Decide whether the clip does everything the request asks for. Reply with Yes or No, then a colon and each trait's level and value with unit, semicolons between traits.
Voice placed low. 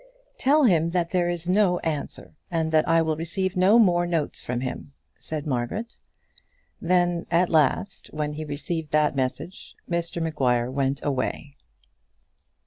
No: medium, 165 Hz